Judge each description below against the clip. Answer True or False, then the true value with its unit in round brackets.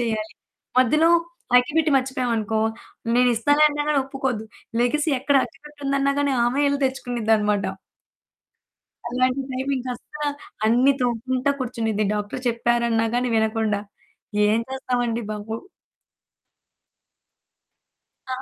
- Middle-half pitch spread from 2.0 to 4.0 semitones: True (3.4 semitones)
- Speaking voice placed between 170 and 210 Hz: False (250 Hz)